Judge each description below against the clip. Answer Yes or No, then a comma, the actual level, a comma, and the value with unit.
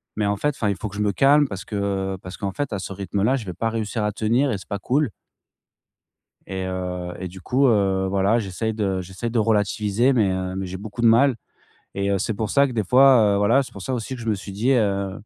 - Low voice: Yes, low, 105 Hz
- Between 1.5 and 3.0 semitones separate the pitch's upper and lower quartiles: No, average, 3.4 semitones